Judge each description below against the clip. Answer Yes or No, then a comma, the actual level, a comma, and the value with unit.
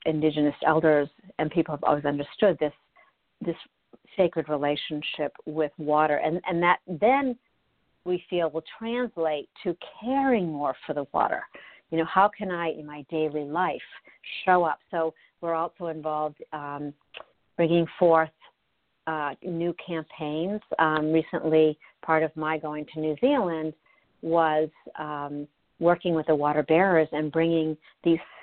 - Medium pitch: Yes, medium, 160 Hz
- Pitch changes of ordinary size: No, narrow, 2.1 semitones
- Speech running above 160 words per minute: No, average, 140 wpm